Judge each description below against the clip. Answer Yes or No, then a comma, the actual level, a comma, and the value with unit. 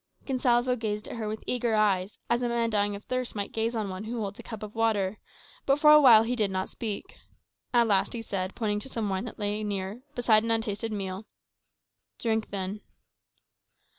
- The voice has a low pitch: No, high, 220 Hz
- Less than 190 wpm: No, fast, 205 wpm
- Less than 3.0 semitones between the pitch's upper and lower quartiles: Yes, narrow, 2.6 semitones